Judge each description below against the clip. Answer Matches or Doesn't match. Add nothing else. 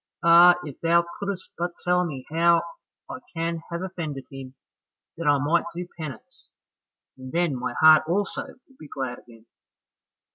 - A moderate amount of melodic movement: Matches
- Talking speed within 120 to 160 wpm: Matches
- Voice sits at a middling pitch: Matches